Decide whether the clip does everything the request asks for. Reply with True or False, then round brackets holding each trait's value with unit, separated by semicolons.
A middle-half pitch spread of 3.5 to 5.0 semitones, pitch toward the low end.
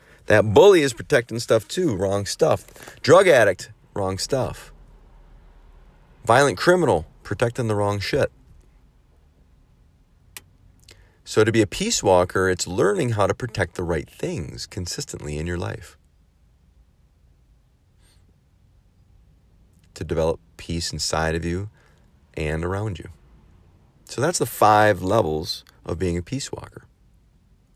True (4.6 semitones; 90 Hz)